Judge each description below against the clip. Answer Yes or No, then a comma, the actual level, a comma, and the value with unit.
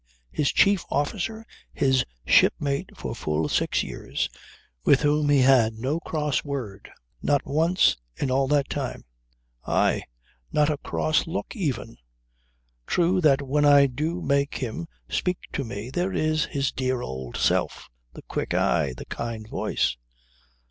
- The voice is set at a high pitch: No, medium, 140 Hz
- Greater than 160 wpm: No, average, 145 wpm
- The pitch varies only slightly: No, average, 3.5 semitones